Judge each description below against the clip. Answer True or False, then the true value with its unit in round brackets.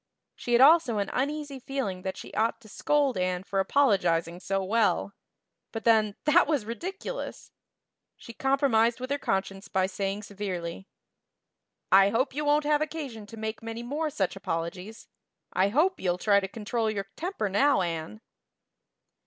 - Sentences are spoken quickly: False (160 wpm)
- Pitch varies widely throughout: True (6.2 semitones)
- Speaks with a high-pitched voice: True (220 Hz)